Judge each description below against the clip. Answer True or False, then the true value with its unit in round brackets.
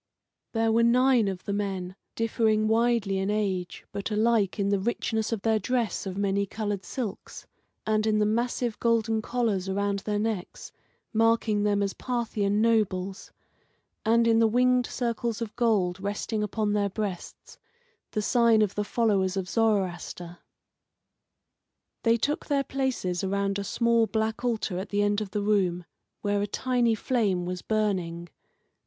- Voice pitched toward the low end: False (215 Hz)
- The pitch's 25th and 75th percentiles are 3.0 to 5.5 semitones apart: False (2.6 semitones)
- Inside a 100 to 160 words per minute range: True (155 wpm)